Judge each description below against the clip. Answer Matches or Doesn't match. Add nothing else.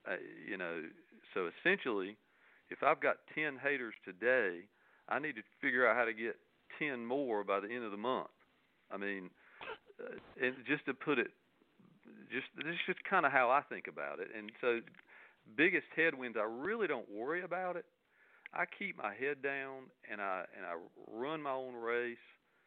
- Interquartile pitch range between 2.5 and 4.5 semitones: Doesn't match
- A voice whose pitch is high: Doesn't match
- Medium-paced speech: Matches